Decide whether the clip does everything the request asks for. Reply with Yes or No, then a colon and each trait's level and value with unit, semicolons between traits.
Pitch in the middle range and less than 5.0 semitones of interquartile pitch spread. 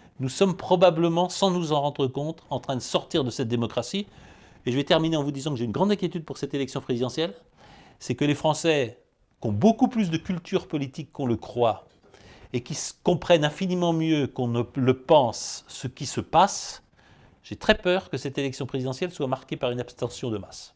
No: medium, 145 Hz; average, 5.3 semitones